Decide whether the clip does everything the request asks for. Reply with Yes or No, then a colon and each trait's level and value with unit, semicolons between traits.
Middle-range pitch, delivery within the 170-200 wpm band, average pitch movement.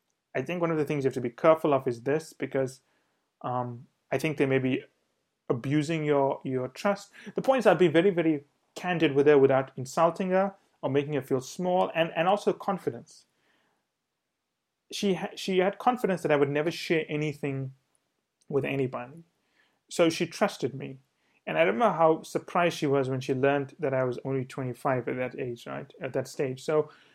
Yes: medium, 150 Hz; average, 195 wpm; average, 4.6 semitones